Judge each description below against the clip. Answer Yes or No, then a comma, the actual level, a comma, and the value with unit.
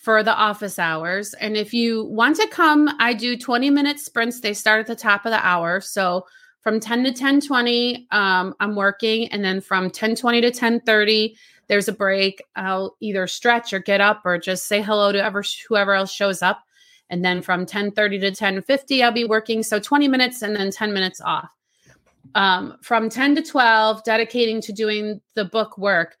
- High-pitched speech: Yes, high, 215 Hz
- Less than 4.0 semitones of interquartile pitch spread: Yes, average, 3.2 semitones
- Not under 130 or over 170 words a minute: No, average, 200 wpm